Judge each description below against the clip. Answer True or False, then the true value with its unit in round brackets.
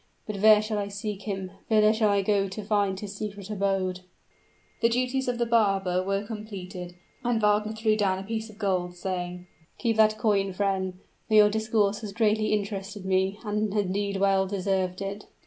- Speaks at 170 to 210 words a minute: True (185 wpm)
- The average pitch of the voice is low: False (205 Hz)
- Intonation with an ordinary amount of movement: False (2.0 semitones)